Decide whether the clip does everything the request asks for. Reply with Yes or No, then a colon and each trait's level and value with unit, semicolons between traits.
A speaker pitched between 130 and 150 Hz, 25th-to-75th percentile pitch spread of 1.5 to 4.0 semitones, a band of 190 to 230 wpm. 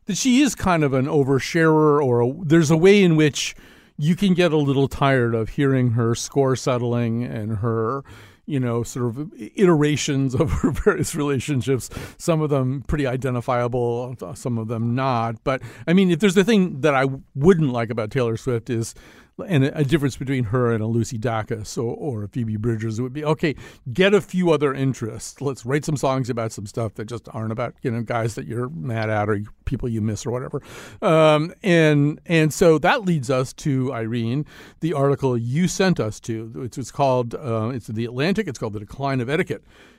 No: low, 135 Hz; average, 4.6 semitones; average, 200 wpm